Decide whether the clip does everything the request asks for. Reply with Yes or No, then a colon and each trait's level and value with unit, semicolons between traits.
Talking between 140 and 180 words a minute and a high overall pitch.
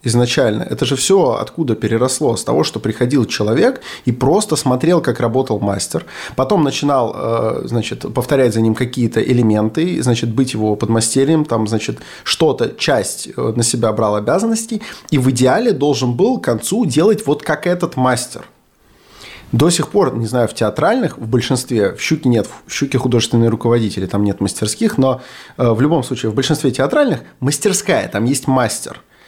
No: fast, 160 wpm; low, 125 Hz